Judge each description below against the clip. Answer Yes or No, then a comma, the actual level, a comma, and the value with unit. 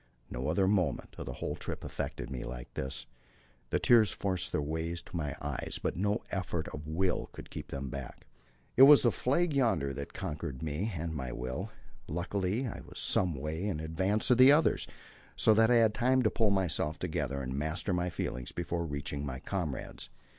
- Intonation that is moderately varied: No, wide, 6.4 semitones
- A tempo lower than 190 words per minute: No, average, 195 wpm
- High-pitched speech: No, very low, 85 Hz